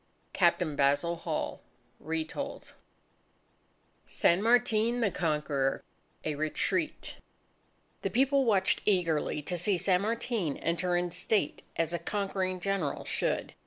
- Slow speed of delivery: Yes, slow, 115 wpm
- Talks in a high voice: No, medium, 180 Hz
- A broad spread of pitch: No, average, 4.6 semitones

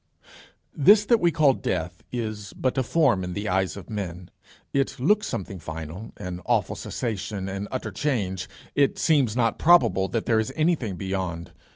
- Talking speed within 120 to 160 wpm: No, average, 170 wpm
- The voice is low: Yes, low, 110 Hz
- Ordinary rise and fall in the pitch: No, wide, 6.6 semitones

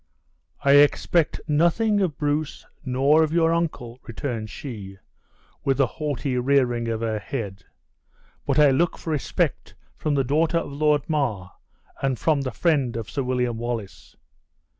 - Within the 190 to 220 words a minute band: No, average, 150 wpm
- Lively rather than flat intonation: No, average, 4.2 semitones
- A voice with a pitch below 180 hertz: Yes, medium, 140 Hz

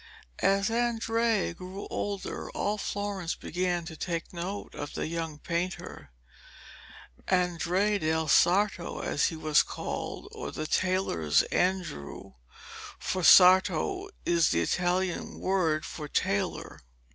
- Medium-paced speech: No, slow, 115 wpm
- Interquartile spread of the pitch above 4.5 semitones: No, average, 3.4 semitones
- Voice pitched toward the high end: No, medium, 180 Hz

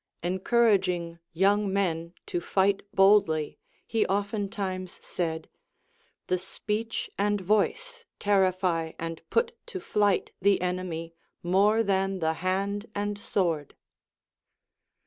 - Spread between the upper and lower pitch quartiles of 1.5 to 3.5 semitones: Yes, average, 2.7 semitones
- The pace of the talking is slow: Yes, slow, 105 wpm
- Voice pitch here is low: No, high, 195 Hz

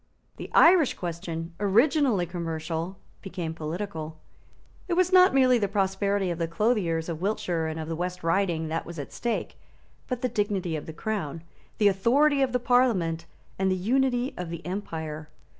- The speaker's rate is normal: Yes, average, 170 wpm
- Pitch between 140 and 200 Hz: Yes, medium, 185 Hz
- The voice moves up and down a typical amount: No, wide, 6.0 semitones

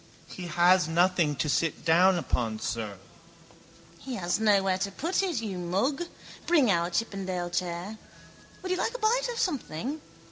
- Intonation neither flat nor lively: No, wide, 7.4 semitones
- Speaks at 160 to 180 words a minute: Yes, average, 165 wpm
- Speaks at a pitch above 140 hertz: Yes, medium, 185 Hz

